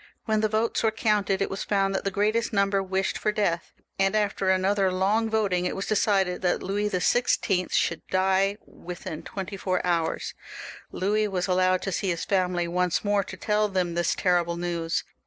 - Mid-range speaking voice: No, high, 195 Hz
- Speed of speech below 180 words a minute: No, average, 185 wpm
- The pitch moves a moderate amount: No, narrow, 2.3 semitones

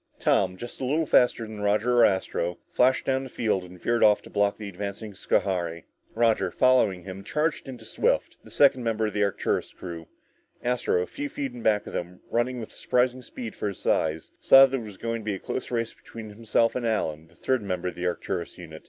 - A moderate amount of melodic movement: Yes, average, 4.8 semitones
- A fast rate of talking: Yes, fast, 220 wpm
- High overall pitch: No, low, 110 Hz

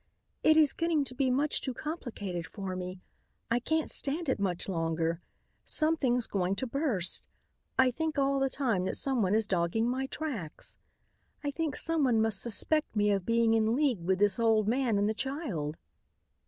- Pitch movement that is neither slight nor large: No, wide, 6.1 semitones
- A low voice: No, high, 235 Hz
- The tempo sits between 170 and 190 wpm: Yes, average, 175 wpm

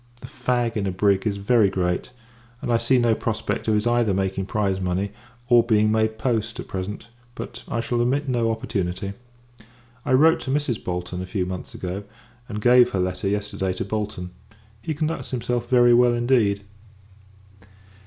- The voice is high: No, low, 110 Hz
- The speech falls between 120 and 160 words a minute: No, average, 175 wpm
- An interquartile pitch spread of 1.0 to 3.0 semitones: No, average, 3.8 semitones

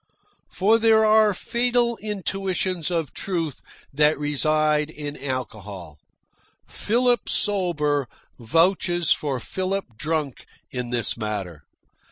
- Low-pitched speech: No, medium, 160 Hz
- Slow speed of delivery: Yes, slow, 100 wpm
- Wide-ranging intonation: Yes, wide, 6.5 semitones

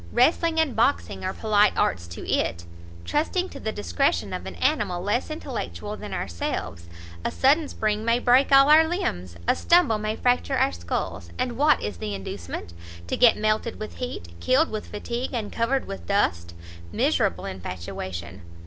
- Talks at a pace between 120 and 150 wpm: No, average, 165 wpm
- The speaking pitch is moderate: No, high, 215 Hz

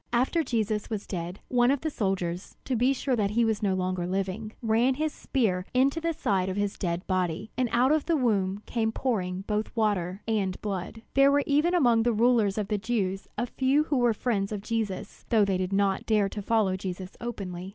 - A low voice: No, high, 215 Hz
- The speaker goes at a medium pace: No, fast, 215 wpm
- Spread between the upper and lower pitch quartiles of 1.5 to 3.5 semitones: No, average, 4.2 semitones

